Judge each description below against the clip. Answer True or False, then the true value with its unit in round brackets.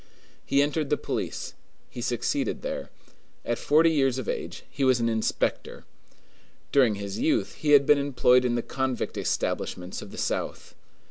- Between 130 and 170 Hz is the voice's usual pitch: True (135 Hz)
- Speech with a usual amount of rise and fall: True (3.5 semitones)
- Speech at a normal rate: True (160 wpm)